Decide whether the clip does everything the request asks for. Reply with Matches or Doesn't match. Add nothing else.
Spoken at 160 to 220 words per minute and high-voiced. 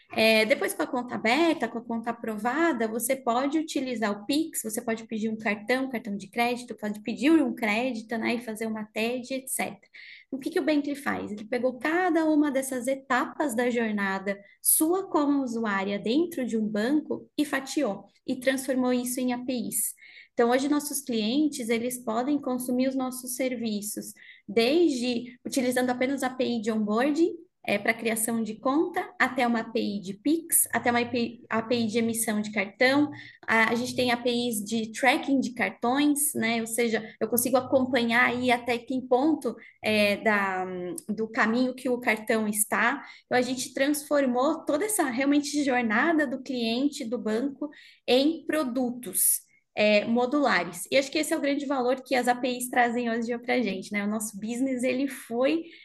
Matches